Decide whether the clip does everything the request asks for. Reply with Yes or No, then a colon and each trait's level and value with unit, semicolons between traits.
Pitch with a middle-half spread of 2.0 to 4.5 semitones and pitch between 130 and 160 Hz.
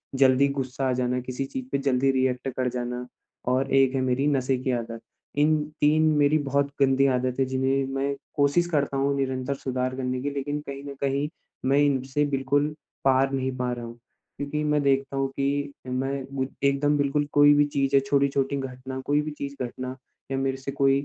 No: narrow, 1.5 semitones; low, 135 Hz